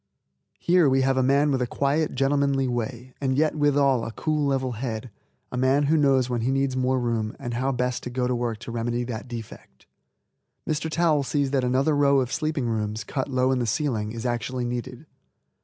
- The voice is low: Yes, low, 130 Hz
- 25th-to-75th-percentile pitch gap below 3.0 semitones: Yes, narrow, 2.6 semitones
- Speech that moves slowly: No, fast, 205 wpm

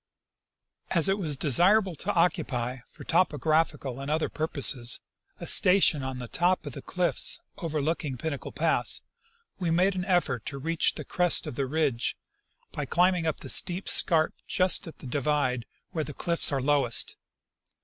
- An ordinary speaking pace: Yes, average, 160 wpm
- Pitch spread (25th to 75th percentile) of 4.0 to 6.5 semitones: Yes, average, 4.4 semitones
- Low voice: No, medium, 155 Hz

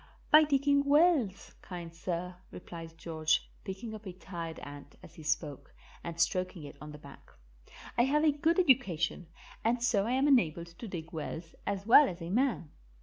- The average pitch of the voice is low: No, medium, 185 Hz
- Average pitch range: No, wide, 7.1 semitones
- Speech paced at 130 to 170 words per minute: No, average, 180 wpm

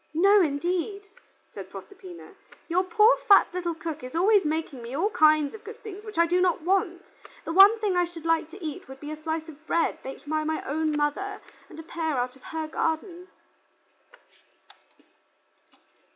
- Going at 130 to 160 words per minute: No, average, 180 wpm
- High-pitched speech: Yes, very high, 335 Hz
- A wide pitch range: No, average, 3.7 semitones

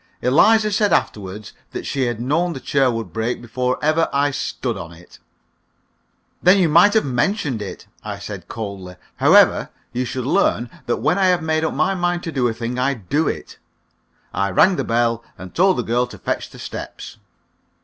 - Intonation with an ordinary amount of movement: No, wide, 6.5 semitones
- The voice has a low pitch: Yes, low, 125 Hz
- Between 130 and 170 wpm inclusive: No, average, 190 wpm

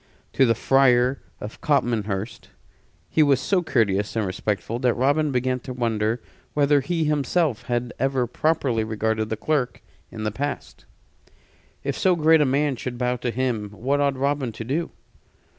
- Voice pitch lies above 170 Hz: No, low, 125 Hz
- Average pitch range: Yes, average, 4.0 semitones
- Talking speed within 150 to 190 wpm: Yes, average, 160 wpm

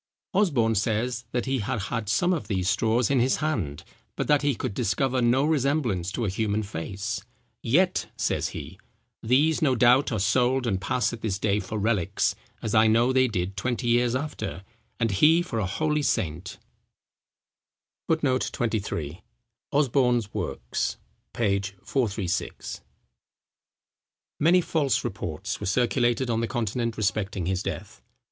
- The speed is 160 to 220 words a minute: No, average, 150 wpm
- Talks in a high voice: No, low, 115 Hz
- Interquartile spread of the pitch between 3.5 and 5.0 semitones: Yes, average, 4.5 semitones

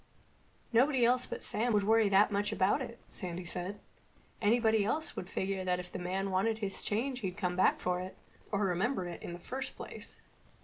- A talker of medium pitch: No, high, 200 Hz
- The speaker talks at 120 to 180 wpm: No, average, 190 wpm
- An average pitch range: Yes, average, 3.9 semitones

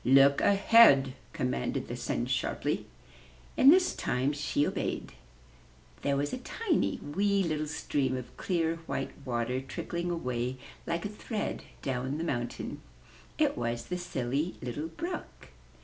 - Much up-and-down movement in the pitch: Yes, wide, 5.7 semitones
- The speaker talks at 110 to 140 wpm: Yes, slow, 135 wpm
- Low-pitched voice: No, medium, 145 Hz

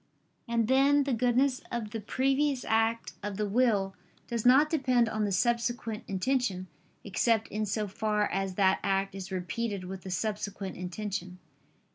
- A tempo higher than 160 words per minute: No, average, 155 wpm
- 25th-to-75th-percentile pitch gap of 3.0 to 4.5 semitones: Yes, average, 3.9 semitones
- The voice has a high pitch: Yes, high, 215 Hz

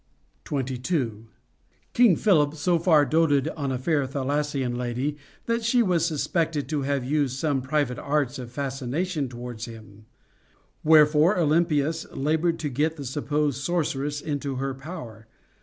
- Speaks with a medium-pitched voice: Yes, medium, 145 Hz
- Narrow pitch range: No, average, 3.4 semitones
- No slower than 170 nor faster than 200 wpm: No, average, 140 wpm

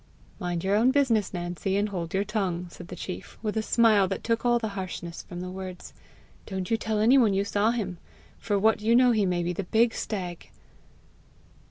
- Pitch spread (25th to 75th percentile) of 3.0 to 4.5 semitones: Yes, average, 3.5 semitones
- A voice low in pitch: No, high, 200 Hz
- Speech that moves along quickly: Yes, fast, 210 wpm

